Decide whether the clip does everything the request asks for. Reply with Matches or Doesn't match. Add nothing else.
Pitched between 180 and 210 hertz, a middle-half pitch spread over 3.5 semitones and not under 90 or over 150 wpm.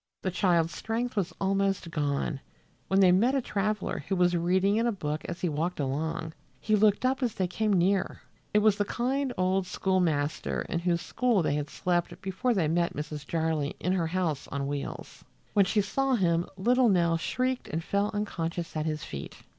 Doesn't match